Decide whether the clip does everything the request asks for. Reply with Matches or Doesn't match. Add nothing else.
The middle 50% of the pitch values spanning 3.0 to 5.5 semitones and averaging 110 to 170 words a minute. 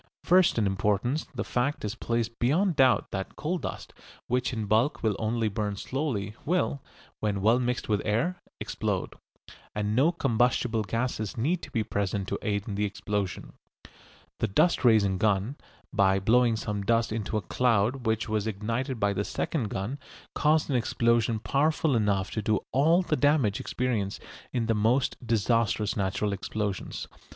Matches